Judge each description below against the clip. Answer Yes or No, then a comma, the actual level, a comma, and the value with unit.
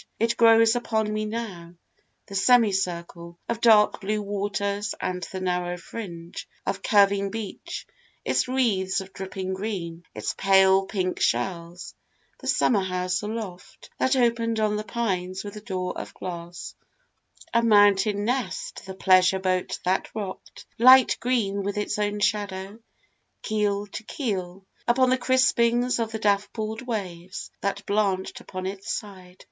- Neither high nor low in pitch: No, high, 200 Hz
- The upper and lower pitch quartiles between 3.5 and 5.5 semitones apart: No, average, 2.9 semitones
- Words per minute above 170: No, average, 140 wpm